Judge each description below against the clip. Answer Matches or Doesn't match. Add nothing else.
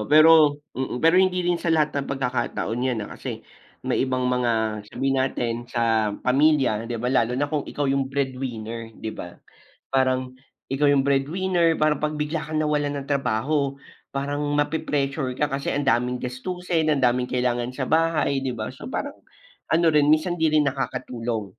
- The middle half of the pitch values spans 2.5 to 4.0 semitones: Matches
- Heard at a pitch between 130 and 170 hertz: Matches